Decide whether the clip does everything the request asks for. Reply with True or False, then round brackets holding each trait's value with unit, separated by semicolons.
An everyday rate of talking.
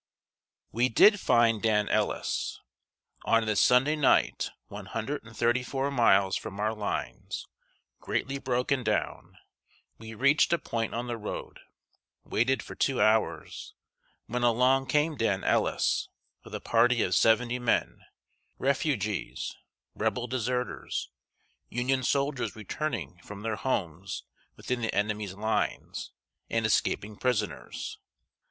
False (125 wpm)